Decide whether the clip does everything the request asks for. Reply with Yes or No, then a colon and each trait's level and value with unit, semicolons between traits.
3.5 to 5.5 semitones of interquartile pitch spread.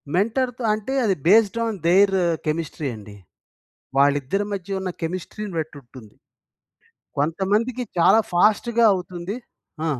Yes: average, 5.2 semitones